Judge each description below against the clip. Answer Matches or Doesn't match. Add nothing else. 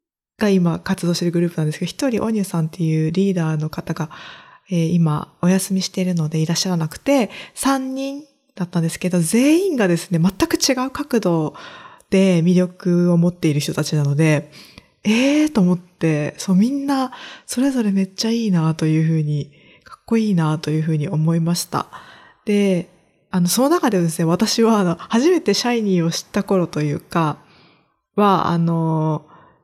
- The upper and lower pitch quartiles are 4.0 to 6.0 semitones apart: Matches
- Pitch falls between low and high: Matches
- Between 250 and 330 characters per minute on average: Doesn't match